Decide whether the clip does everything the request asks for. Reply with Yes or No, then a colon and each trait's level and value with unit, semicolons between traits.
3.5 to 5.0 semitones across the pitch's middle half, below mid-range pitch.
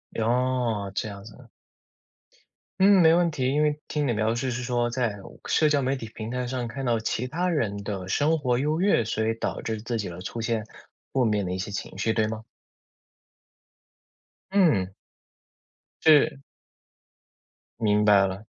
Yes: average, 4.5 semitones; low, 120 Hz